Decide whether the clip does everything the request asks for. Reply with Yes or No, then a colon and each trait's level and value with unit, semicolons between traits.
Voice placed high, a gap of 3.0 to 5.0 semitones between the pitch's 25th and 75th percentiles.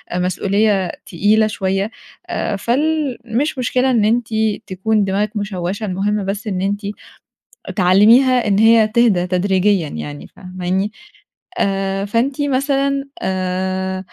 Yes: high, 205 Hz; average, 3.5 semitones